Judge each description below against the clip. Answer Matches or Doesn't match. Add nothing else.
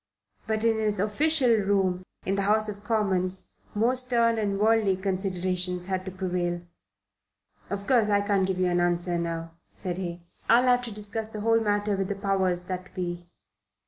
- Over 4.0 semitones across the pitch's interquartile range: Doesn't match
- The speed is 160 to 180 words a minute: Matches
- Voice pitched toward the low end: Doesn't match